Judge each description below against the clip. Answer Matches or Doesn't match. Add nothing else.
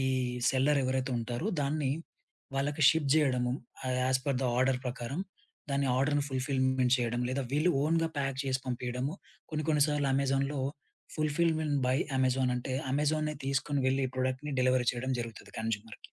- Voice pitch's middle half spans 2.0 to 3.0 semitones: Matches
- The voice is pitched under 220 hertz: Matches